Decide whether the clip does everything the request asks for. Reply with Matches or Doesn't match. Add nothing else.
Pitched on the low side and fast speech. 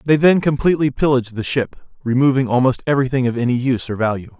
Doesn't match